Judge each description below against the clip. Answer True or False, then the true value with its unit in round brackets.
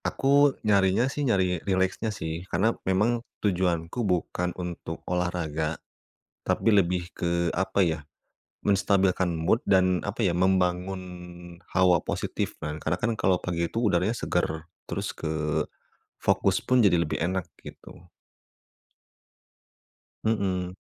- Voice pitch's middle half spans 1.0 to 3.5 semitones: True (2.5 semitones)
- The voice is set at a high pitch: False (90 Hz)